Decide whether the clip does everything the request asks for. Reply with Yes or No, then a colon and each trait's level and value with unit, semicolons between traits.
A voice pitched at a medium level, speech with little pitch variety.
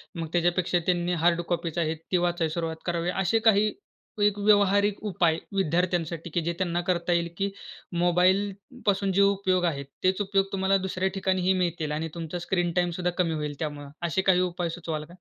Yes: medium, 175 Hz; narrow, 2.1 semitones